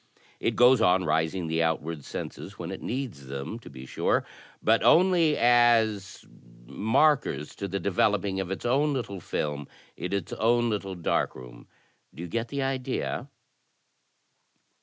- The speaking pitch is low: Yes, low, 100 Hz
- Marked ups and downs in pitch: Yes, wide, 6.5 semitones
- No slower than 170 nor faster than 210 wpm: No, average, 140 wpm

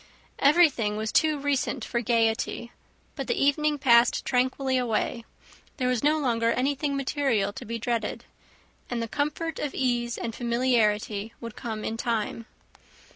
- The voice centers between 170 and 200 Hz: No, high, 245 Hz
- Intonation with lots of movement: No, average, 3.5 semitones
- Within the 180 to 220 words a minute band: No, average, 145 wpm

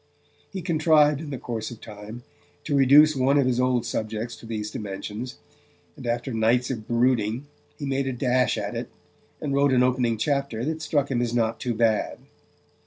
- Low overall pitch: Yes, low, 125 Hz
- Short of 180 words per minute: No, average, 185 wpm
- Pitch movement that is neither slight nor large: Yes, average, 3.5 semitones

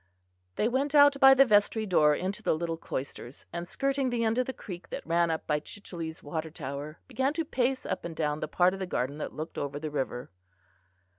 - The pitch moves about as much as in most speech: No, wide, 8.5 semitones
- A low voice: No, medium, 175 Hz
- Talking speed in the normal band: No, fast, 220 wpm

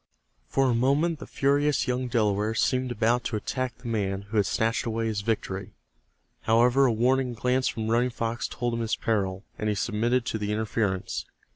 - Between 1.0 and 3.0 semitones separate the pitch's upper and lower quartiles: Yes, average, 2.7 semitones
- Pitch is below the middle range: Yes, low, 115 Hz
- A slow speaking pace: No, average, 185 wpm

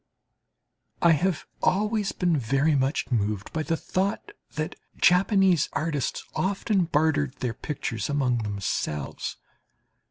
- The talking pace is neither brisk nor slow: No, slow, 115 wpm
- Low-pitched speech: No, medium, 155 Hz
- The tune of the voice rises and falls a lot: Yes, wide, 6.1 semitones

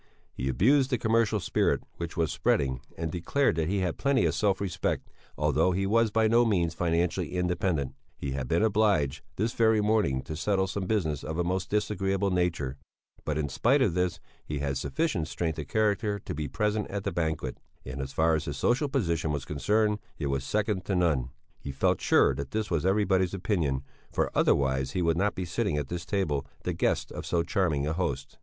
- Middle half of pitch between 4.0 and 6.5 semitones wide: Yes, wide, 5.6 semitones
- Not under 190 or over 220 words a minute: Yes, fast, 205 wpm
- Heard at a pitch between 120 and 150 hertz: No, very low, 90 Hz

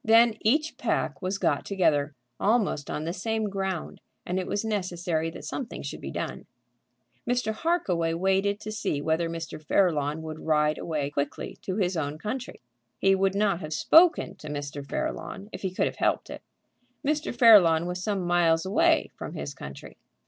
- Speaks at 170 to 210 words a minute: Yes, average, 175 wpm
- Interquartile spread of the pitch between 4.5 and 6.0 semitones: Yes, average, 4.9 semitones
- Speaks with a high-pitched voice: No, medium, 180 Hz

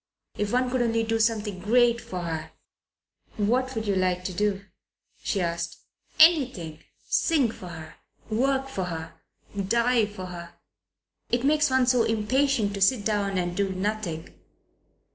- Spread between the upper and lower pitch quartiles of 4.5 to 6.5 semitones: Yes, average, 5.0 semitones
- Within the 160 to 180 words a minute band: No, average, 150 wpm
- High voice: Yes, high, 210 Hz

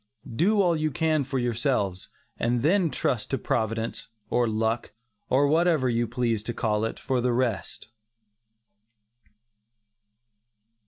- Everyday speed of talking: No, slow, 125 wpm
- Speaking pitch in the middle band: No, low, 125 Hz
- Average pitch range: Yes, average, 4.7 semitones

